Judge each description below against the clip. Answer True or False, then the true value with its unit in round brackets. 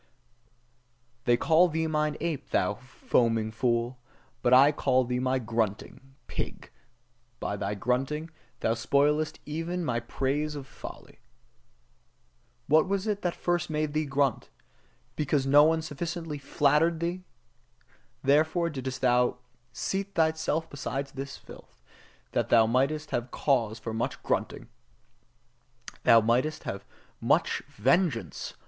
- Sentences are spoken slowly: True (130 wpm)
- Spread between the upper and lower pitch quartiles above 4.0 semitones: True (4.4 semitones)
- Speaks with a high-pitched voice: False (140 Hz)